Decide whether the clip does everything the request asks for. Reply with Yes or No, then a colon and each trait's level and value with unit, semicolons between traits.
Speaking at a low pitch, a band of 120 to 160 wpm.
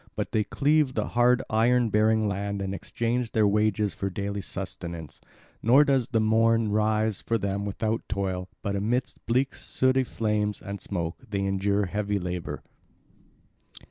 Yes: low, 105 Hz; average, 150 wpm